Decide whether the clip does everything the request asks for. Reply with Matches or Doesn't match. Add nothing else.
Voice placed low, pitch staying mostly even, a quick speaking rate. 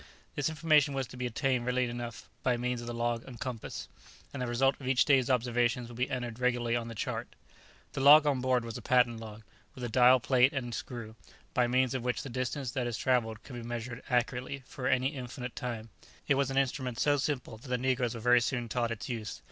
Matches